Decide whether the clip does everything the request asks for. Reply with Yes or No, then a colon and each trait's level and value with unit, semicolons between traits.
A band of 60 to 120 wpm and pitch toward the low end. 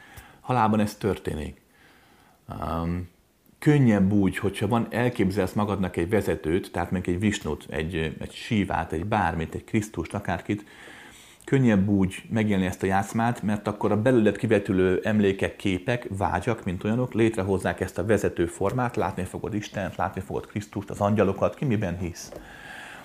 No: average, 145 wpm; low, 100 Hz